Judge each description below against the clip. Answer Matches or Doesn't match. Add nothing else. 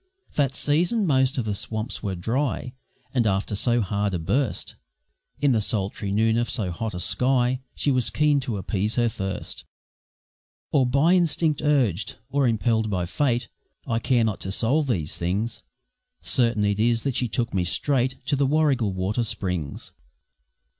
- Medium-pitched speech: Doesn't match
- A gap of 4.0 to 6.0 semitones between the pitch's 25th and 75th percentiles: Matches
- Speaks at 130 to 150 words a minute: Doesn't match